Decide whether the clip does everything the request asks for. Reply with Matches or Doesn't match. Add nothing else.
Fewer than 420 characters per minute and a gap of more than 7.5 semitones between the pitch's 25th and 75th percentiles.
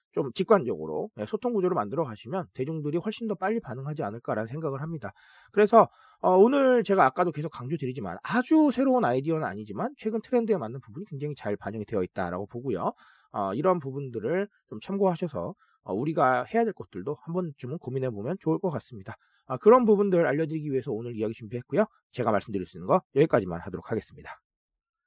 Doesn't match